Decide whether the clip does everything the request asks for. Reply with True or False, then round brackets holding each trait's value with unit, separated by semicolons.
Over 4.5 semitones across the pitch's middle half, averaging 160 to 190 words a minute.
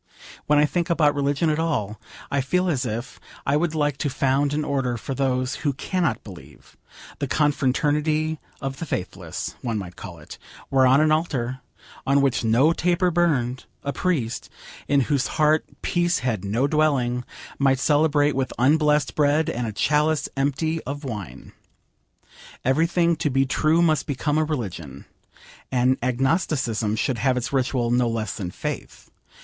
False (3.7 semitones; 165 wpm)